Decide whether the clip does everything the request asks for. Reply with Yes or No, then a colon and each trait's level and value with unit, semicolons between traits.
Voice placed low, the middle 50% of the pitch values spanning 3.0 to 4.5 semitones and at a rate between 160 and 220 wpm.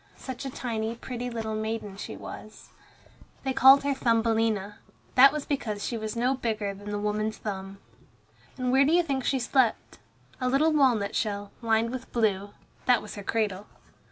No: high, 225 Hz; average, 3.6 semitones; average, 175 wpm